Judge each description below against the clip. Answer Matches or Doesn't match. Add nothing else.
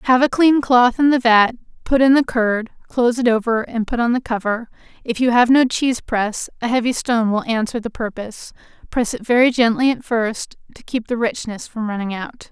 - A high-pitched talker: Matches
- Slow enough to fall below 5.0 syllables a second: Doesn't match